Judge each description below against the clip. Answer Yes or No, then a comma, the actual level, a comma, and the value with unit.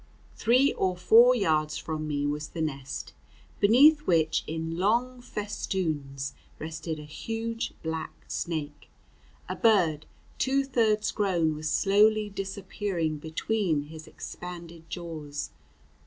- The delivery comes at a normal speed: No, slow, 115 wpm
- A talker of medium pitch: Yes, medium, 170 Hz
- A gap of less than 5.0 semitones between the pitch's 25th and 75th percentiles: No, wide, 5.4 semitones